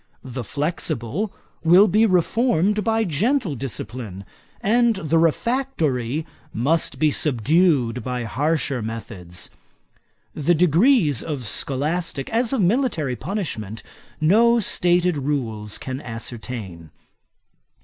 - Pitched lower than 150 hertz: No, medium, 155 Hz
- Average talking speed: No, slow, 100 wpm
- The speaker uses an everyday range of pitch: No, wide, 7.6 semitones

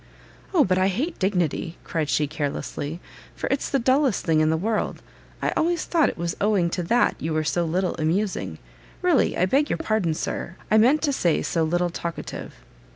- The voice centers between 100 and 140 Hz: No, medium, 185 Hz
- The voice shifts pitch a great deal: Yes, wide, 6.9 semitones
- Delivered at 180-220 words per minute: Yes, average, 195 wpm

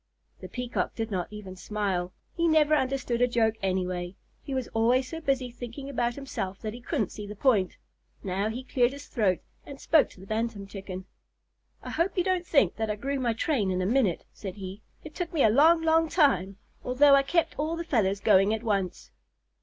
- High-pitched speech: Yes, high, 235 Hz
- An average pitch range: No, wide, 6.0 semitones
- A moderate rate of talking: No, fast, 210 wpm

